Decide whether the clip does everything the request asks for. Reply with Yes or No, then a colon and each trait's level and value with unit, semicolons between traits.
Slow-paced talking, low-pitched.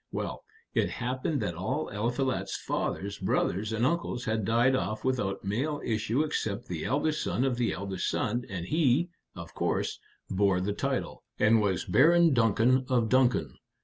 No: average, 160 wpm; low, 115 Hz